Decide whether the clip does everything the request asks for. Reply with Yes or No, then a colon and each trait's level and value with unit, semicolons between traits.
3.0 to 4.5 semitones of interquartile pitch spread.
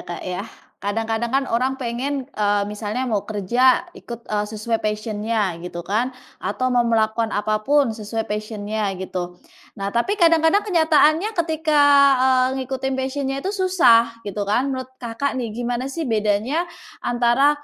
Yes: average, 4.0 semitones